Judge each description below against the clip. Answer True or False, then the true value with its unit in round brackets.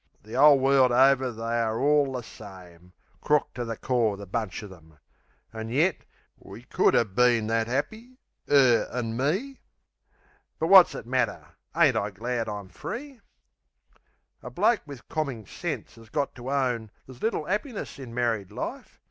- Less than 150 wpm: False (165 wpm)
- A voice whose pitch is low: True (125 Hz)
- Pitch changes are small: False (4.2 semitones)